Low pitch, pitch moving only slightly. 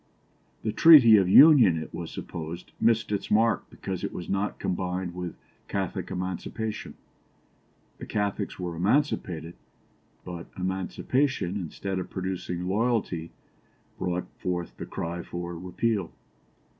No: very low, 95 Hz; average, 3.7 semitones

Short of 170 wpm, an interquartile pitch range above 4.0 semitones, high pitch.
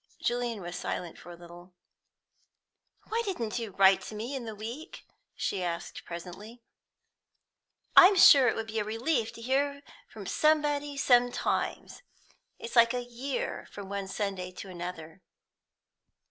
Yes: average, 145 wpm; wide, 5.4 semitones; high, 225 Hz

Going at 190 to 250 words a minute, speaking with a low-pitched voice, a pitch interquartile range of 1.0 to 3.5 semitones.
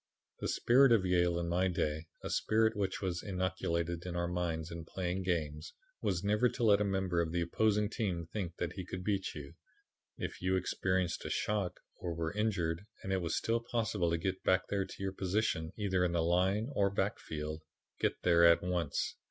Yes: average, 195 wpm; very low, 90 Hz; average, 2.9 semitones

